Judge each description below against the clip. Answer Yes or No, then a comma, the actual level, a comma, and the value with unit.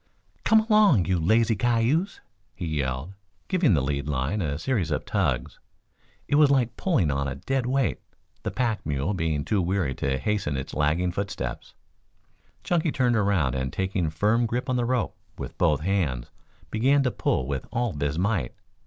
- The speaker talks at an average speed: Yes, average, 170 wpm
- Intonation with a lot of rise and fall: Yes, wide, 8.8 semitones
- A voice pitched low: Yes, very low, 95 Hz